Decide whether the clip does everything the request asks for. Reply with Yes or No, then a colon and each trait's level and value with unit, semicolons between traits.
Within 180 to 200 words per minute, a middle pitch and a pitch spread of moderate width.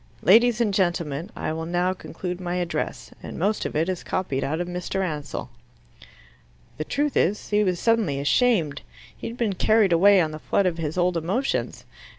Yes: average, 185 wpm; medium, 180 Hz; average, 4.1 semitones